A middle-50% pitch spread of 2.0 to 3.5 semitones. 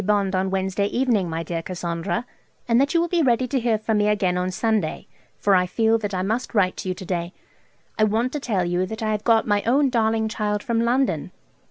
No: average, 3.9 semitones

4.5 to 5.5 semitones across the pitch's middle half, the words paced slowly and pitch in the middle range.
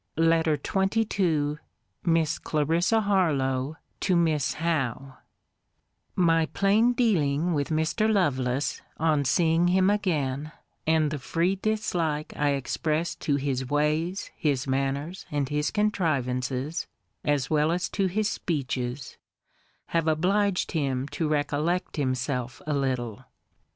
No: average, 4.0 semitones; slow, 115 wpm; medium, 155 Hz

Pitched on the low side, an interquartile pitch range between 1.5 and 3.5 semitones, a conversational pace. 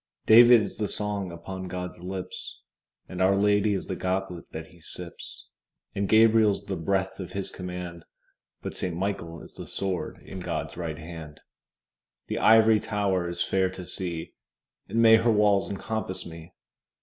Yes: very low, 95 Hz; average, 2.9 semitones; average, 160 wpm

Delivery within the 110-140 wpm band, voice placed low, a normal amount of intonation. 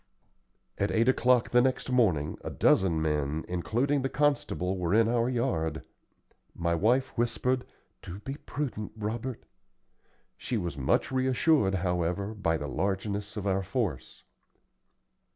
No: slow, 135 wpm; low, 105 Hz; wide, 6.1 semitones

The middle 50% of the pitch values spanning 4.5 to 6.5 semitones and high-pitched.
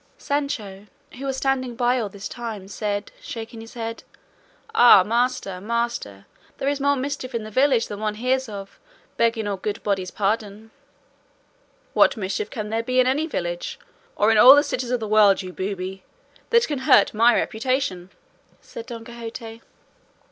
No: average, 3.8 semitones; high, 225 Hz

